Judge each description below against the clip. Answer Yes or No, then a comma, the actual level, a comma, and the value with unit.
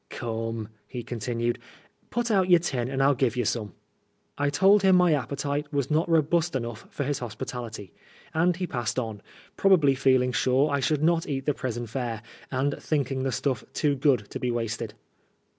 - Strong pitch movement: No, average, 4.0 semitones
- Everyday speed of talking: Yes, average, 190 wpm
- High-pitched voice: No, low, 135 Hz